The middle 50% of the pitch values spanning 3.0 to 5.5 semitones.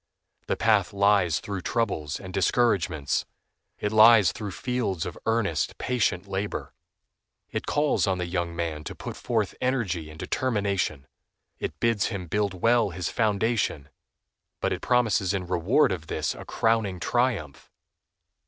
Yes: average, 4.4 semitones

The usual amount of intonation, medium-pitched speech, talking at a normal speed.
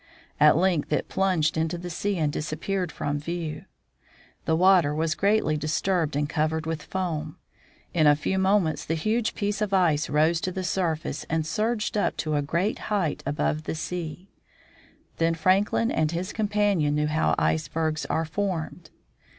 Yes: average, 3.6 semitones; medium, 165 Hz; average, 165 wpm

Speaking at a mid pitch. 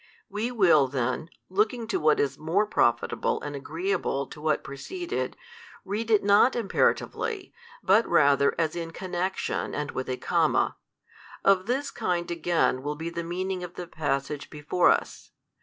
Yes: medium, 175 Hz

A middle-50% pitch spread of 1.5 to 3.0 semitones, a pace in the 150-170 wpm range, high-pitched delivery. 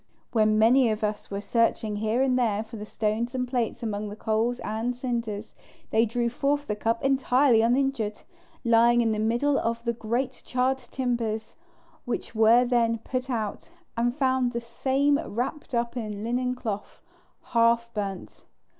Yes: narrow, 2.4 semitones; average, 165 wpm; high, 235 Hz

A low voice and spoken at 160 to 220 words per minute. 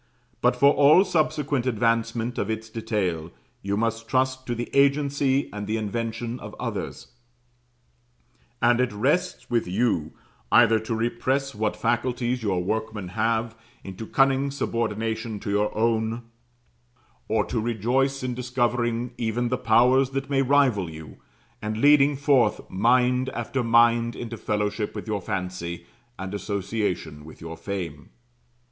No: low, 115 Hz; average, 140 wpm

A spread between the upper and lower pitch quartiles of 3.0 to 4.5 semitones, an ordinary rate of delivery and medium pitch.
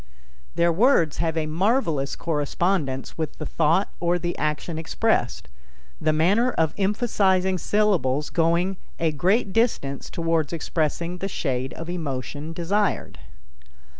No: average, 3.8 semitones; slow, 125 wpm; medium, 165 Hz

